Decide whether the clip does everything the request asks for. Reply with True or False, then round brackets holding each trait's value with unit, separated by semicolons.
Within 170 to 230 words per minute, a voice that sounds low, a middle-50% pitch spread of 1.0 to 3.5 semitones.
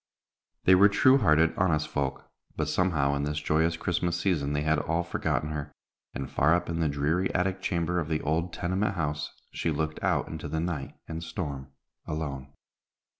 True (180 wpm; 80 Hz; 2.9 semitones)